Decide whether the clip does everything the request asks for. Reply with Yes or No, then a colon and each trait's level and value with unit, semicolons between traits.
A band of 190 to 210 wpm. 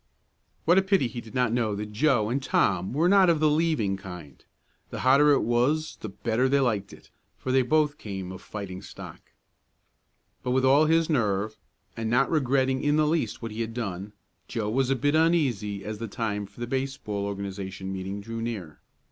Yes: average, 200 wpm